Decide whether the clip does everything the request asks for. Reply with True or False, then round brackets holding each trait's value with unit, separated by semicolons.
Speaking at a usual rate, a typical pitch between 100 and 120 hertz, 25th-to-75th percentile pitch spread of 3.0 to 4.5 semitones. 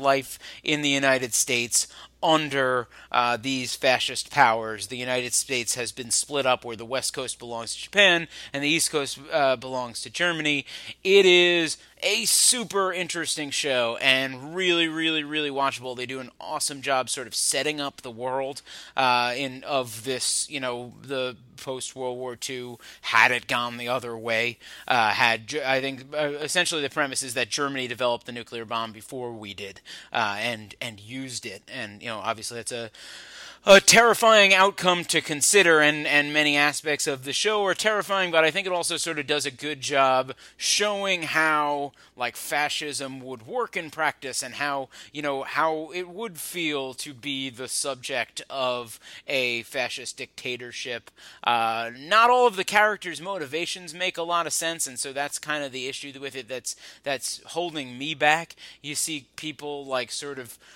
False (180 wpm; 140 Hz; 3.9 semitones)